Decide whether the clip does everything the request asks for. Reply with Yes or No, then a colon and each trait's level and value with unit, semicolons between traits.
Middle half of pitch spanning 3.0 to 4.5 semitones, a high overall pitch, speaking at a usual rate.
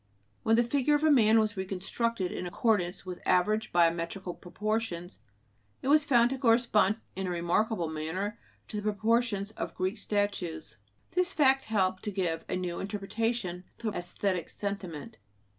Yes: average, 4.2 semitones; high, 205 Hz; average, 155 wpm